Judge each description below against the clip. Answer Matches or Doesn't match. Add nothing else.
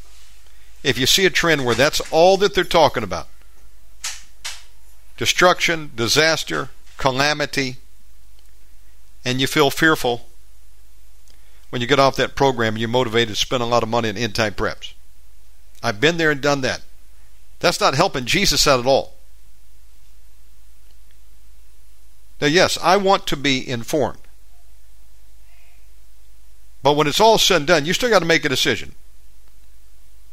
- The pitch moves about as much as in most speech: Doesn't match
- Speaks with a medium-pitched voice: Doesn't match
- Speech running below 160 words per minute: Matches